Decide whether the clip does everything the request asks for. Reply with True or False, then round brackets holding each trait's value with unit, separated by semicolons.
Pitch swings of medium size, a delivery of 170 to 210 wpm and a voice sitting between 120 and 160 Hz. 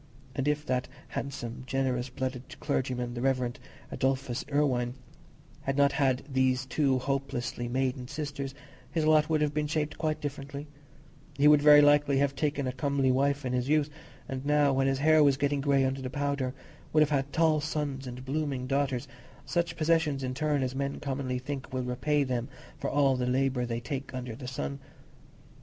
False (2.2 semitones; 180 wpm; 135 Hz)